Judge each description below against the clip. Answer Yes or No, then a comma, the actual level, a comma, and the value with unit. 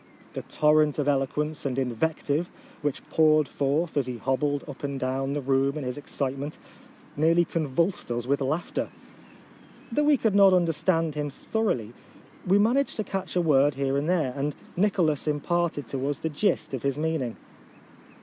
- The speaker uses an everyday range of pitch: Yes, average, 3.6 semitones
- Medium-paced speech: Yes, average, 175 wpm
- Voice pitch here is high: No, medium, 150 Hz